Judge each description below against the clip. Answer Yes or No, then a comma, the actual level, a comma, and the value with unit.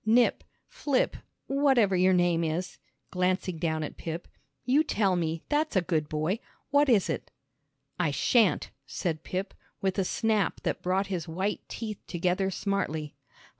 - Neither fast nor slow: Yes, average, 150 wpm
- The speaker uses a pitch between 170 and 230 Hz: Yes, medium, 185 Hz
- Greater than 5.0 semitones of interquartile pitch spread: No, average, 4.2 semitones